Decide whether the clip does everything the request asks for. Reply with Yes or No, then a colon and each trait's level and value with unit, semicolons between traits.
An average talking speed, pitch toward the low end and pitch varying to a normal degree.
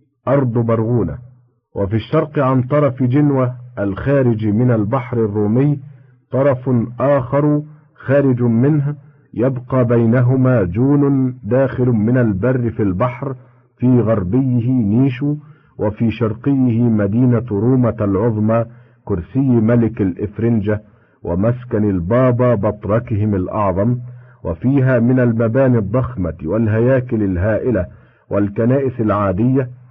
Yes: average, 90 wpm; low, 120 Hz; average, 3.0 semitones